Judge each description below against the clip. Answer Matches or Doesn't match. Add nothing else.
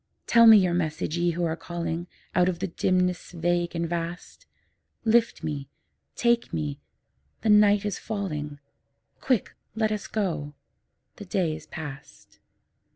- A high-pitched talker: Doesn't match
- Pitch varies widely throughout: Doesn't match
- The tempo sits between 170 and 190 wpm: Doesn't match